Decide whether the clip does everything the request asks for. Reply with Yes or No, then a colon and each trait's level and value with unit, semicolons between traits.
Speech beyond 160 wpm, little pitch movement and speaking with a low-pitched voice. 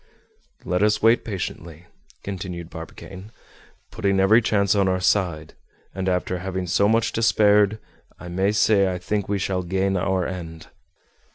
No: average, 150 wpm; narrow, 2.2 semitones; very low, 95 Hz